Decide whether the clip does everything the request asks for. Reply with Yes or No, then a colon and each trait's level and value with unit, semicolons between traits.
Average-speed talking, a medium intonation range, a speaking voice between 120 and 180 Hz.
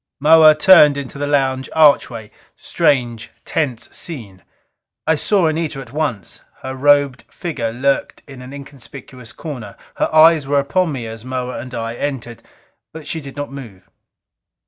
Yes: average, 150 wpm; average, 3.4 semitones; medium, 140 Hz